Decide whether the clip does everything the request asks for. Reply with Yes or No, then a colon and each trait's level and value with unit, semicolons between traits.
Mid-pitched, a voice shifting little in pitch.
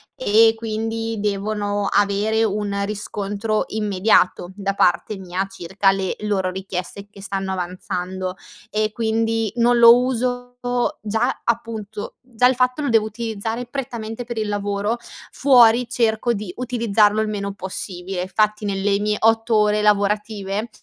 No: high, 210 Hz; narrow, 2.2 semitones